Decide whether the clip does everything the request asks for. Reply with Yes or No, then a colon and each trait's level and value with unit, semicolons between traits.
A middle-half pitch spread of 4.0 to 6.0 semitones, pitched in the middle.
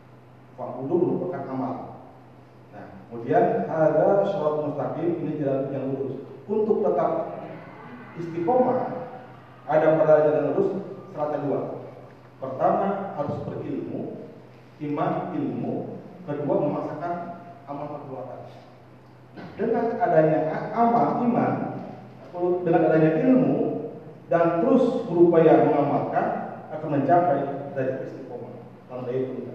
Yes: average, 5.2 semitones; medium, 160 Hz